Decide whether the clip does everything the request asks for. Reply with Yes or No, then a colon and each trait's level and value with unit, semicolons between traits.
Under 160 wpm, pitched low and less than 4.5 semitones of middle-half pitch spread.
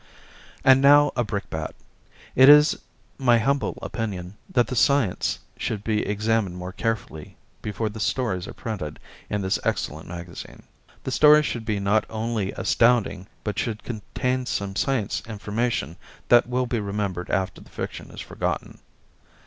Yes: average, 150 wpm; low, 110 Hz; average, 3.9 semitones